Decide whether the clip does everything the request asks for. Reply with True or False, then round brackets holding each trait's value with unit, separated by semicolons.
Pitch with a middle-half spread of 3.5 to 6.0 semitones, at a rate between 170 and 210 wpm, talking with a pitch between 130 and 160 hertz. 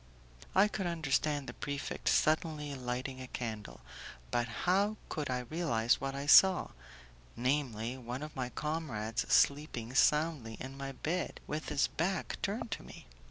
False (4.1 semitones; 150 wpm; 140 Hz)